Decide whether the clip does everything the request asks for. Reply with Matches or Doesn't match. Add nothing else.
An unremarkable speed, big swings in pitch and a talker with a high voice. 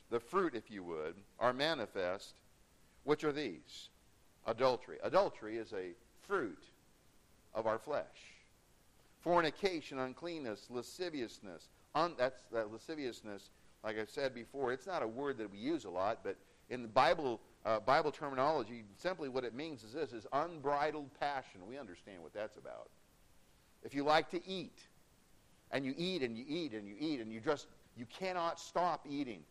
Doesn't match